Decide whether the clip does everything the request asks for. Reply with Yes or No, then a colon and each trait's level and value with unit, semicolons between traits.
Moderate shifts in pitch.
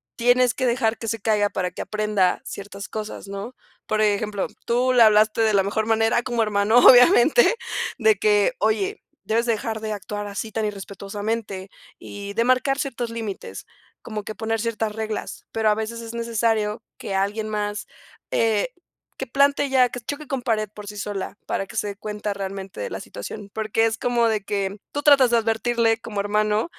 No: narrow, 2.1 semitones